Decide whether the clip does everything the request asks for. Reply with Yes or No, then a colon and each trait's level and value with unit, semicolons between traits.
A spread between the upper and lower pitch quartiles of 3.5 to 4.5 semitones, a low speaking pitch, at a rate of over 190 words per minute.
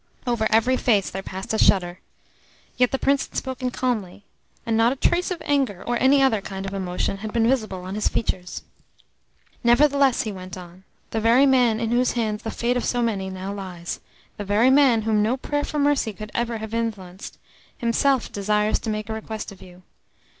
No: average, 4.1 semitones; high, 220 Hz; average, 200 wpm